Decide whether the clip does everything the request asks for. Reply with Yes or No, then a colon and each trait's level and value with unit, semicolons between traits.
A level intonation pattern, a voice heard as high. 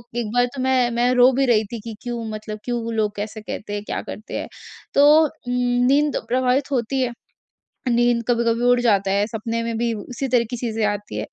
Yes: narrow, 2.2 semitones; high, 235 Hz